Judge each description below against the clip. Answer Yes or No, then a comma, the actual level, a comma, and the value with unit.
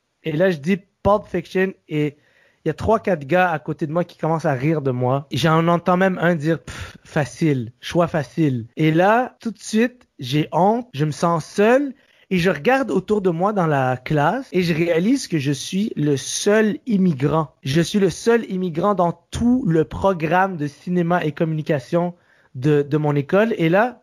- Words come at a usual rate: Yes, average, 200 wpm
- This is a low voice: No, medium, 170 Hz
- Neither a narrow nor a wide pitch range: Yes, average, 4.3 semitones